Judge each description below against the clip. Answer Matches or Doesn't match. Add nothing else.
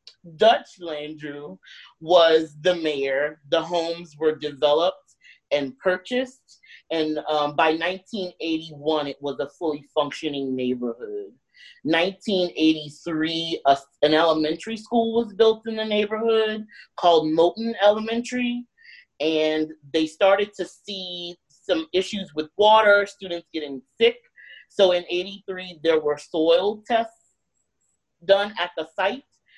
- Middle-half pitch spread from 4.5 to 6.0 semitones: Matches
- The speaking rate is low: Matches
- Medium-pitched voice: Matches